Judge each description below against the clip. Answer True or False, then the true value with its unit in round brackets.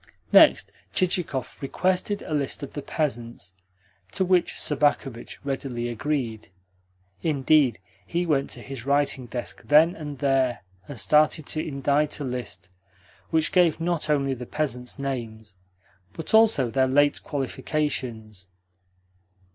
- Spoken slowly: True (125 wpm)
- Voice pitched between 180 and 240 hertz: False (140 Hz)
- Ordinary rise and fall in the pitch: True (3.6 semitones)